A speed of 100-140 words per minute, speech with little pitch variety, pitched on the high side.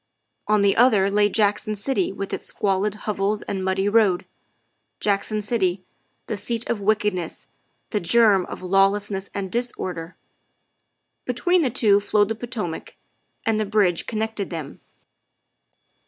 Yes: slow, 135 wpm; narrow, 2.2 semitones; high, 205 Hz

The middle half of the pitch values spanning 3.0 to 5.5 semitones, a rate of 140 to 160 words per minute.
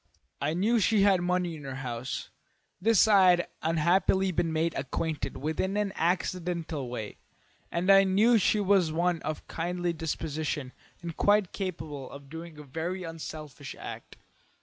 Yes: average, 3.4 semitones; average, 150 wpm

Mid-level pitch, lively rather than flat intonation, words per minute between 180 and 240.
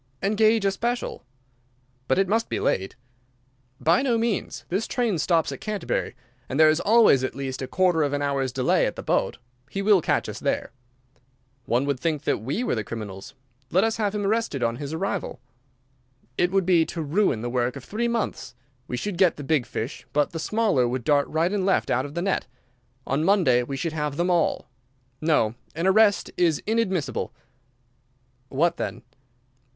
Yes: medium, 165 Hz; wide, 6.6 semitones; average, 190 wpm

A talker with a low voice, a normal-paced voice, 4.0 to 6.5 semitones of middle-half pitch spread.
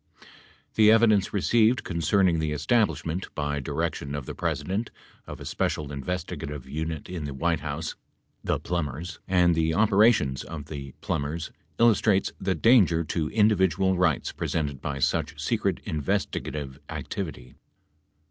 No: very low, 80 Hz; slow, 130 wpm; average, 4.8 semitones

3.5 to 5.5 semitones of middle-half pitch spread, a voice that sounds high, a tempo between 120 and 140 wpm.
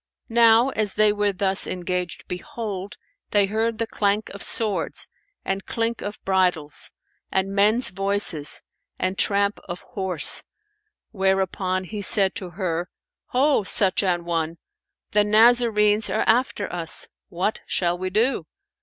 No: average, 2.8 semitones; high, 200 Hz; slow, 135 wpm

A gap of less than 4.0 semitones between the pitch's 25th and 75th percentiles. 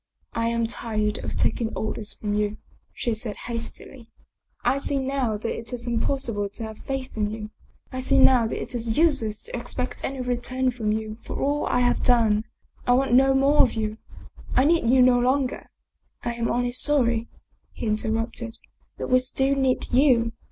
Yes: average, 2.8 semitones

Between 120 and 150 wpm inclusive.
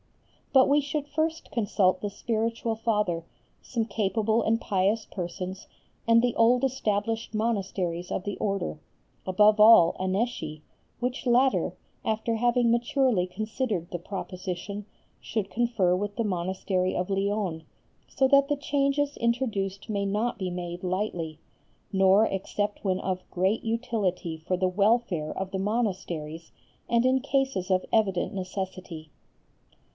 Yes: slow, 135 wpm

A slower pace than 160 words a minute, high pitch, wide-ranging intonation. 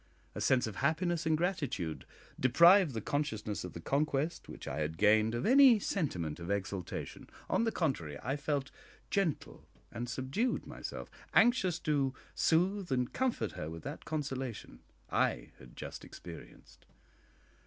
No: average, 145 wpm; low, 135 Hz; wide, 8.3 semitones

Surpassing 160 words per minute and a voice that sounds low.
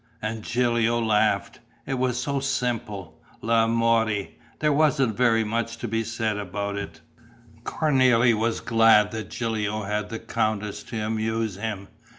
No: average, 140 wpm; low, 115 Hz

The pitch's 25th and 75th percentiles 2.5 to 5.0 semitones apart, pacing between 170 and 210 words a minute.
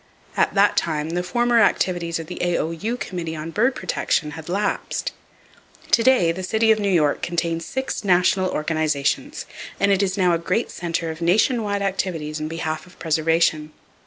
Yes: average, 3.7 semitones; average, 175 wpm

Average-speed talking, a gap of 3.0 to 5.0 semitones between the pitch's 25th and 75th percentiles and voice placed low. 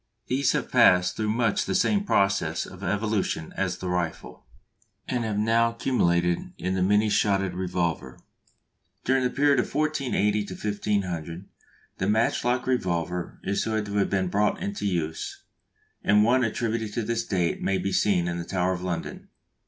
Yes: average, 160 wpm; average, 4.2 semitones; low, 100 Hz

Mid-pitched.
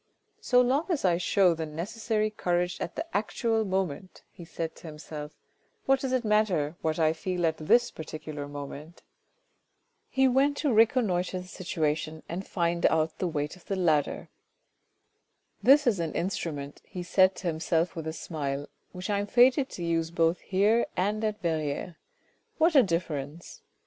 Yes: medium, 175 Hz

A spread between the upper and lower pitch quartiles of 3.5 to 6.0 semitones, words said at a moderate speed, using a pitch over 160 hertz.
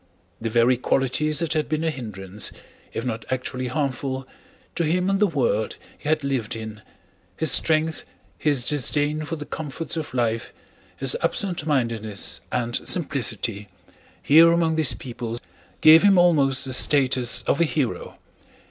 No: average, 4.9 semitones; average, 145 wpm; low, 135 Hz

